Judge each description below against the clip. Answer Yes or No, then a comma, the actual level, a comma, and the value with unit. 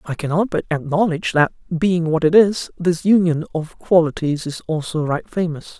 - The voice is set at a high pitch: No, medium, 165 Hz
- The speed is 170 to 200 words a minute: Yes, average, 175 wpm